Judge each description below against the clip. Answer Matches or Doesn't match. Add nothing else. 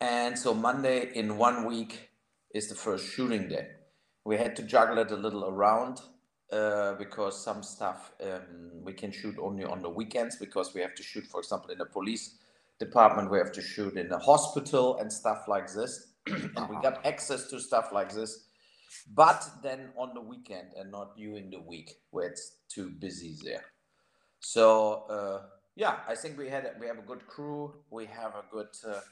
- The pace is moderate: Matches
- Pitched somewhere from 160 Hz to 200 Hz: Doesn't match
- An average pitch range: Matches